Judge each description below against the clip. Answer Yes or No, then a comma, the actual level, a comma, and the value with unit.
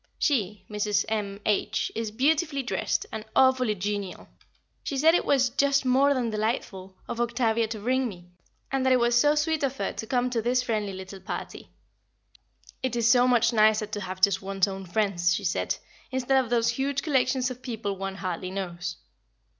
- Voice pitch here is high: Yes, high, 230 Hz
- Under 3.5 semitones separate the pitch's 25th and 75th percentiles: No, average, 4.3 semitones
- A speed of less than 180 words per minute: No, average, 185 wpm